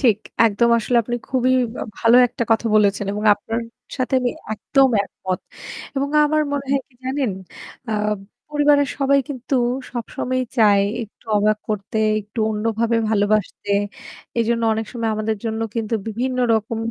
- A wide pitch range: No, average, 3.2 semitones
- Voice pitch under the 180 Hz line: No, high, 230 Hz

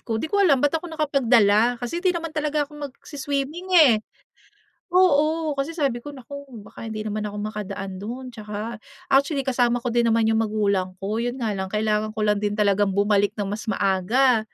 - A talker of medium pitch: No, high, 235 Hz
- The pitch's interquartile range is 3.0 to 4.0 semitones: No, average, 5.1 semitones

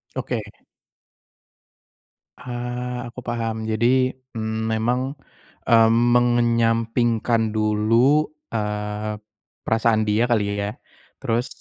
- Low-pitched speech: Yes, low, 115 Hz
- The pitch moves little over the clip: Yes, narrow, 1.8 semitones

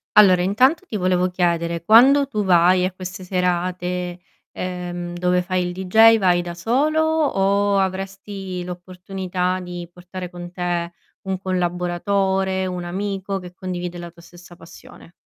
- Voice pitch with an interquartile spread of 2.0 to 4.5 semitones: No, narrow, 1.6 semitones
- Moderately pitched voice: Yes, medium, 180 Hz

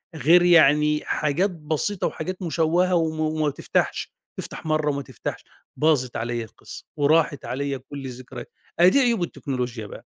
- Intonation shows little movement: No, average, 3.8 semitones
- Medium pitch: Yes, medium, 150 Hz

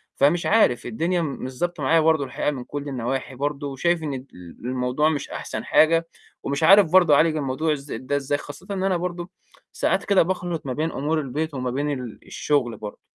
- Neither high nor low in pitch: Yes, medium, 145 Hz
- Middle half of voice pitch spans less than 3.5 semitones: No, average, 3.8 semitones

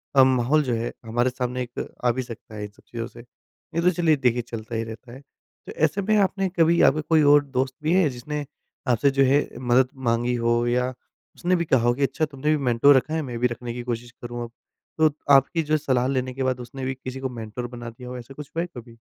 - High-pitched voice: No, low, 130 Hz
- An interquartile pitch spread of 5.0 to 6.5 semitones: No, average, 3.5 semitones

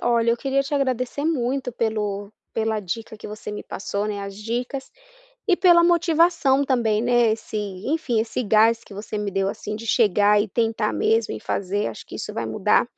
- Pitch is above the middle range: Yes, high, 225 Hz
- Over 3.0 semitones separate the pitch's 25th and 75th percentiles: Yes, average, 3.8 semitones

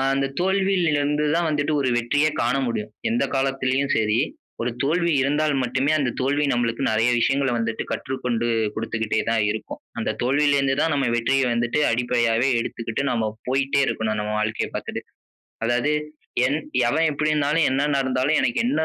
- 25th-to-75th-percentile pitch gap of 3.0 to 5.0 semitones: Yes, average, 3.9 semitones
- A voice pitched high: No, low, 135 Hz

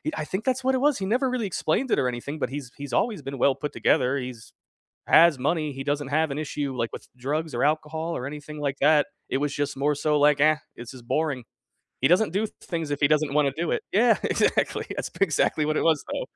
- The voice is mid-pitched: Yes, medium, 150 Hz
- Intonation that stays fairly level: No, average, 3.0 semitones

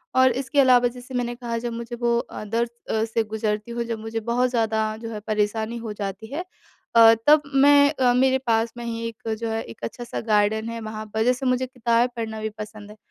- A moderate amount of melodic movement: No, narrow, 1.9 semitones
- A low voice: No, high, 230 Hz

